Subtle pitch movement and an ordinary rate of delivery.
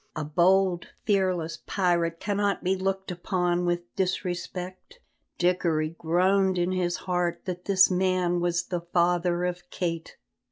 No: narrow, 1.3 semitones; slow, 130 wpm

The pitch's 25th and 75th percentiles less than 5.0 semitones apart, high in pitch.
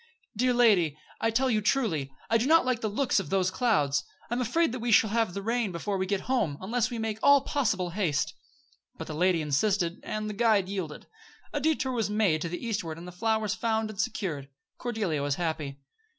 No: average, 5.3 semitones; high, 210 Hz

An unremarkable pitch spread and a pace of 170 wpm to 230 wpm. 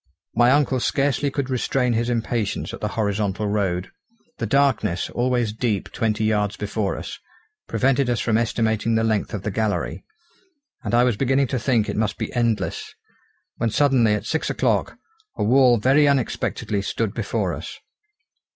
No: average, 3.3 semitones; average, 160 wpm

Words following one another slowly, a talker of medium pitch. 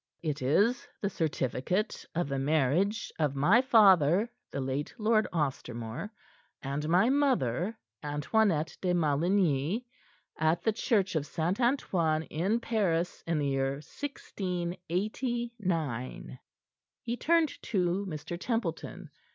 Yes: slow, 115 wpm; medium, 175 Hz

